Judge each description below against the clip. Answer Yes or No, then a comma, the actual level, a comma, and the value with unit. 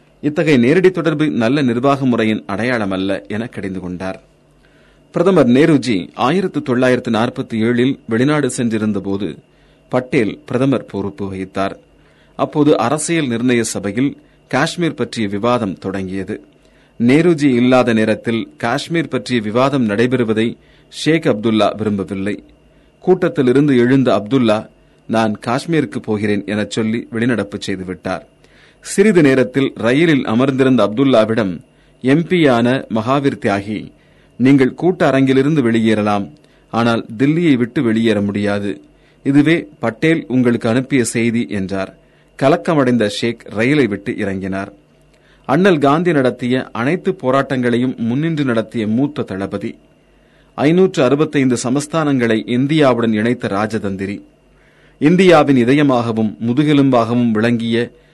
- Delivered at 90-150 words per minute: Yes, average, 100 wpm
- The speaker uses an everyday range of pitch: Yes, average, 4.5 semitones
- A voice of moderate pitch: No, low, 120 Hz